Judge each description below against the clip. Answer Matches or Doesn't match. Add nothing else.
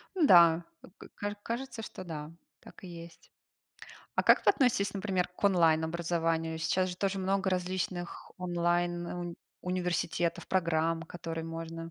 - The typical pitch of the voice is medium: Matches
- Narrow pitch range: Matches